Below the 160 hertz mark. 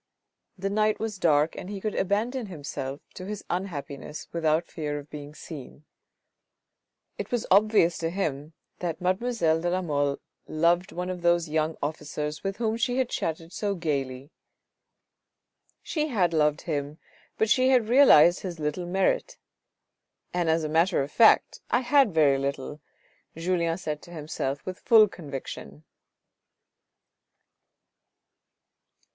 No: medium, 170 Hz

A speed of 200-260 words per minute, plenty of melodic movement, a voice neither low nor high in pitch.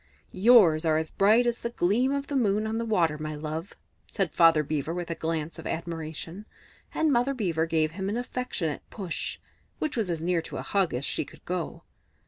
Yes: fast, 205 wpm; wide, 5.7 semitones; medium, 175 Hz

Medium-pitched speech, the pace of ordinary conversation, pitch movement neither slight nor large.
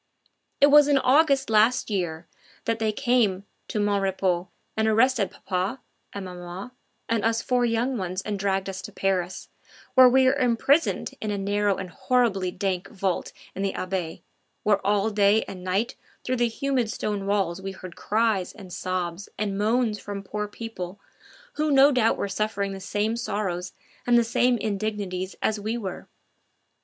No: high, 205 Hz; average, 170 wpm; average, 3.4 semitones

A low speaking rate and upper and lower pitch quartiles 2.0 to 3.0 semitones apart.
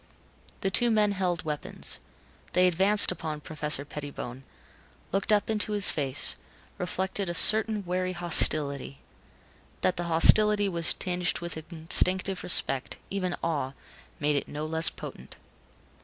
No: slow, 130 wpm; average, 4.2 semitones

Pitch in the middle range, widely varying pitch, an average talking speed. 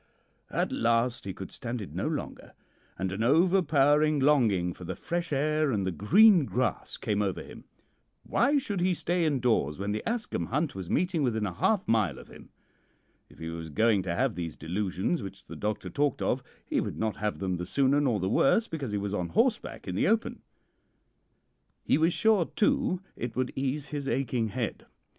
No: low, 125 Hz; wide, 7.7 semitones; average, 195 wpm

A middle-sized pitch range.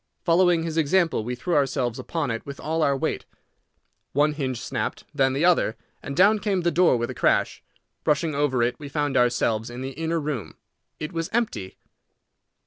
Yes: average, 4.5 semitones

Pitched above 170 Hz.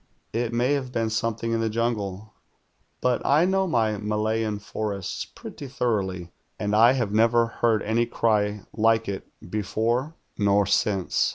No: low, 110 Hz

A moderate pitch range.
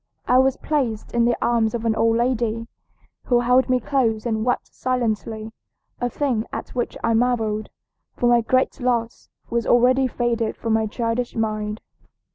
No: narrow, 1.9 semitones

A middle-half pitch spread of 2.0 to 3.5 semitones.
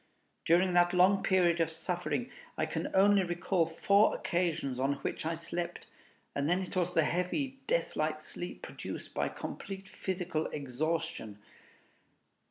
Yes: narrow, 2.6 semitones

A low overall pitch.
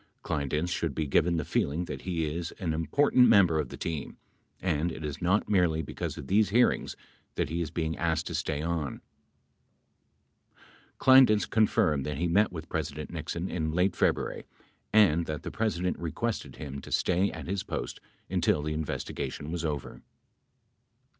Yes: very low, 85 Hz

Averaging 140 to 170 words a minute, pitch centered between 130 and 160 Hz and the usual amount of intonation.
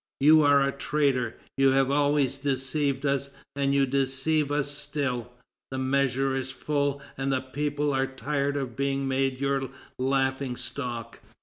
No: average, 150 wpm; low, 135 Hz; narrow, 1.3 semitones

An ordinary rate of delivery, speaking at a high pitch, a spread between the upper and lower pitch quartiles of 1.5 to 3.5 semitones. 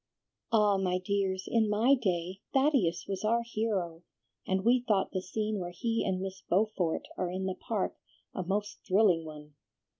Yes: average, 170 wpm; high, 195 Hz; average, 2.9 semitones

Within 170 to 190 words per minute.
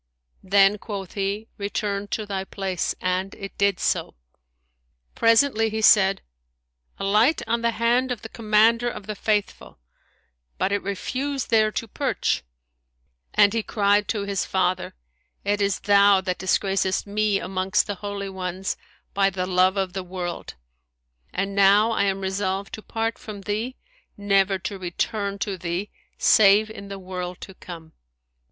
No: average, 150 wpm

